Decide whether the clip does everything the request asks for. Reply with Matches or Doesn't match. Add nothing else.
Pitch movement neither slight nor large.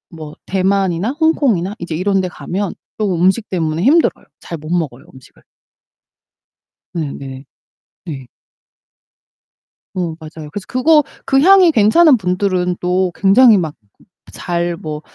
Matches